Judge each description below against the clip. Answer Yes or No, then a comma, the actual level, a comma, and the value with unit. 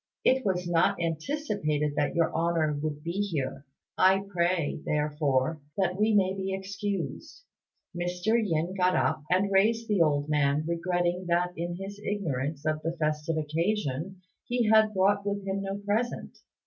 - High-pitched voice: No, medium, 175 Hz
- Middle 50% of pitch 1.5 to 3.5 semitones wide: No, average, 4.2 semitones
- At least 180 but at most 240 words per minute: No, average, 155 wpm